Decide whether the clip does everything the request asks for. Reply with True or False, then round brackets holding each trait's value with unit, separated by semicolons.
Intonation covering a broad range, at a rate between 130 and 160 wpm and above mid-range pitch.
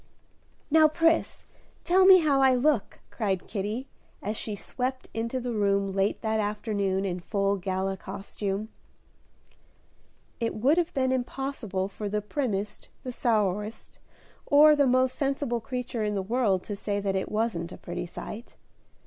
False (4.6 semitones; 150 wpm; 220 Hz)